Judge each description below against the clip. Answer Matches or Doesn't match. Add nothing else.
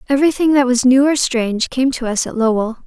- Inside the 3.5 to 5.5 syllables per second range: Doesn't match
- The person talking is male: Doesn't match